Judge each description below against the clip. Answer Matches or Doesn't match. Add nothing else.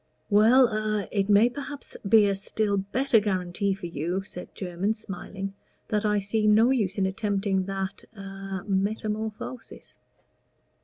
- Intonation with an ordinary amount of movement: Doesn't match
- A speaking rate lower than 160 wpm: Matches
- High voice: Matches